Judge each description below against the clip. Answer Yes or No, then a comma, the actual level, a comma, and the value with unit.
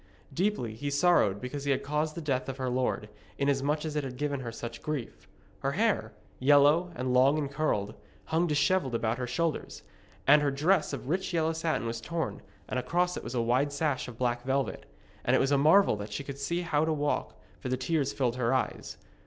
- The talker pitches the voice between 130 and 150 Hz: Yes, medium, 140 Hz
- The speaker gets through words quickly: Yes, fast, 215 wpm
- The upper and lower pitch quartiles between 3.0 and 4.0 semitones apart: Yes, average, 3.6 semitones